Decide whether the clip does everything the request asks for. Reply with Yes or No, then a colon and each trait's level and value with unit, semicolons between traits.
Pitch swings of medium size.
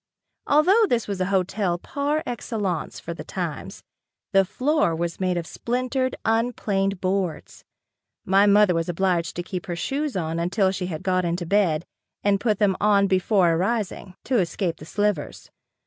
Yes: average, 3.5 semitones